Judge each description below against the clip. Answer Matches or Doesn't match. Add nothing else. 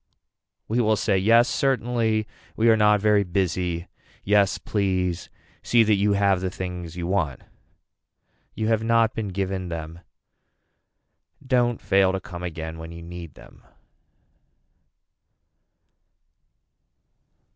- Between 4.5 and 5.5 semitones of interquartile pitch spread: Doesn't match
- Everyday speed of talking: Doesn't match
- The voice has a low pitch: Matches